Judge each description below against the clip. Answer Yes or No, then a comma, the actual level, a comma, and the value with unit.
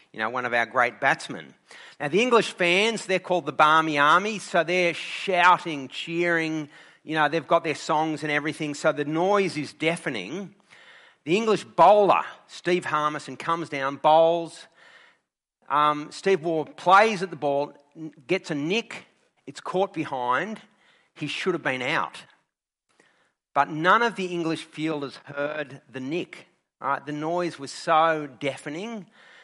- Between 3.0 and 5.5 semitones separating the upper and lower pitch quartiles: Yes, average, 3.4 semitones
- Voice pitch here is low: No, medium, 160 Hz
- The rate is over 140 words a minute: Yes, average, 150 wpm